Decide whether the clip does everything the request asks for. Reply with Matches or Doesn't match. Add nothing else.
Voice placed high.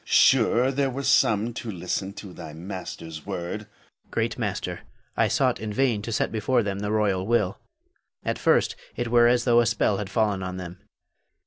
Doesn't match